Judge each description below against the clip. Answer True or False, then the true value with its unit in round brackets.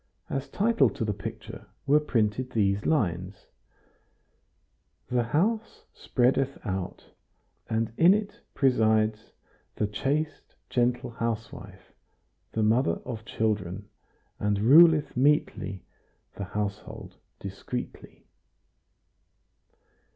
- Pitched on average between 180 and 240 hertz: False (115 Hz)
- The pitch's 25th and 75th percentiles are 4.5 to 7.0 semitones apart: True (4.8 semitones)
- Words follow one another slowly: True (90 wpm)